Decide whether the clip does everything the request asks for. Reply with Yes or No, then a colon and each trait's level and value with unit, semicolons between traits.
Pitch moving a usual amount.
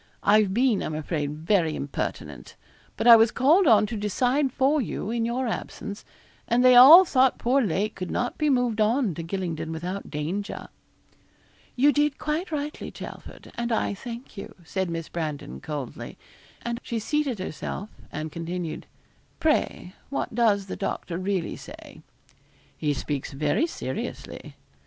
No: wide, 7.0 semitones